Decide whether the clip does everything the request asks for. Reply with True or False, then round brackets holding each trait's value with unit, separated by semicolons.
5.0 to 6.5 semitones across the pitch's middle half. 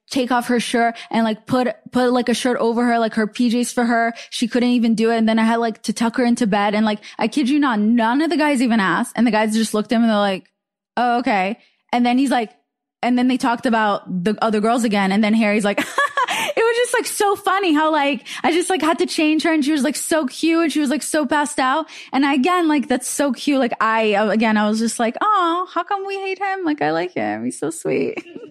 True (5.3 semitones)